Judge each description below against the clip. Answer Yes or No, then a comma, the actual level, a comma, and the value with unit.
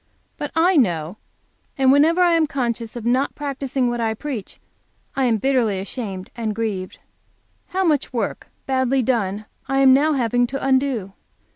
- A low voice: No, very high, 255 Hz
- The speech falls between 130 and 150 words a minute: No, average, 160 wpm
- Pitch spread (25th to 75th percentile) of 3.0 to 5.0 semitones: Yes, average, 3.8 semitones